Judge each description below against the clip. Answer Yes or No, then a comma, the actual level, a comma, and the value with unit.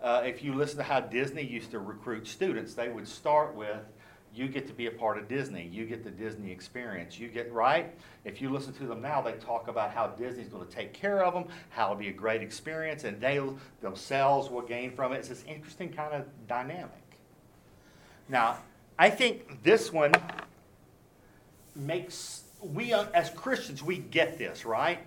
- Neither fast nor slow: Yes, average, 195 wpm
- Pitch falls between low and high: No, low, 130 Hz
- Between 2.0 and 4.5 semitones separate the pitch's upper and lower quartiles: No, average, 5.0 semitones